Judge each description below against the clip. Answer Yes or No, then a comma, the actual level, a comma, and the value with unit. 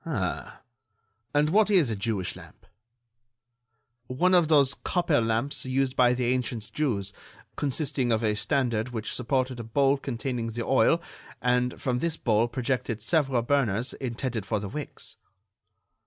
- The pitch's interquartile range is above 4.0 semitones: No, average, 3.6 semitones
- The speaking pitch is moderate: No, low, 125 Hz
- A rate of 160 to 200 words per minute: No, average, 145 wpm